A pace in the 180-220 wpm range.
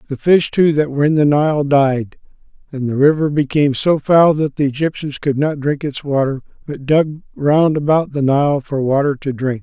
Yes: fast, 205 wpm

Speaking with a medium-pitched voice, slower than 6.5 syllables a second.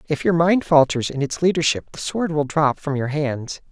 Yes: medium, 150 Hz; 4.9 syllables/s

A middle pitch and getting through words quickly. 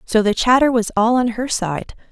No: high, 230 Hz; fast, 225 wpm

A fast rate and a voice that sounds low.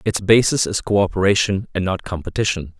No: average, 150 wpm; very low, 95 Hz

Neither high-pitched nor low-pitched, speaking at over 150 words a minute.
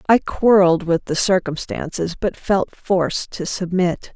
No: medium, 180 Hz; average, 145 wpm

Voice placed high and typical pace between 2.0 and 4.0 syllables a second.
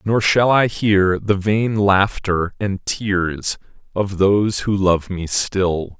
No: very low, 95 Hz; 3.1 syllables/s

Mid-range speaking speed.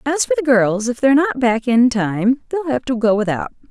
No: fast, 245 wpm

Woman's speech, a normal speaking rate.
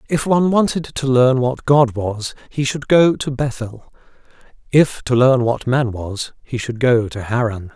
No: male; average, 185 wpm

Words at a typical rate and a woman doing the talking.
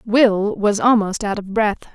Yes: average, 185 wpm; female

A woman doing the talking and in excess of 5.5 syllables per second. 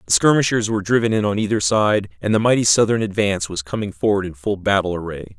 No: male; 6.4 syllables/s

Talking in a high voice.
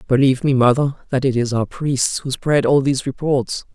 No: low, 135 Hz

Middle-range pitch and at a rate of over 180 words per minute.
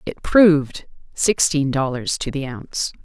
No: medium, 150 Hz; average, 140 wpm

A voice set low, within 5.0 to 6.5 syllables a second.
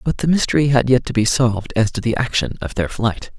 Yes: low, 120 Hz; 6.0 syllables/s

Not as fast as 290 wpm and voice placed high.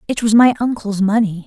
Yes: fast, 205 wpm; high, 220 Hz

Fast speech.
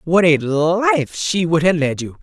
Yes: fast, 215 wpm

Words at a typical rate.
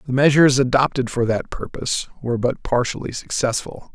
Yes: average, 150 wpm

